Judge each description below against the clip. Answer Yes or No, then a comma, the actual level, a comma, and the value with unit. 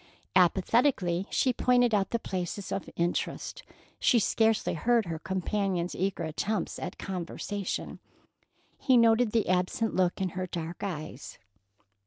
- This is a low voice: No, high, 190 Hz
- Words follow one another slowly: Yes, slow, 130 wpm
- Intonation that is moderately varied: Yes, average, 4.1 semitones